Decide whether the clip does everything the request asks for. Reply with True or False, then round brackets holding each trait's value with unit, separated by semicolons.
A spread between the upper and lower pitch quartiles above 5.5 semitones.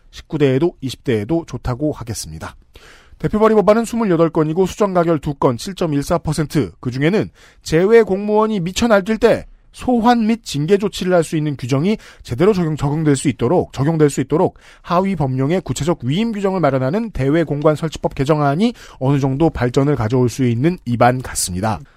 True (6.0 semitones)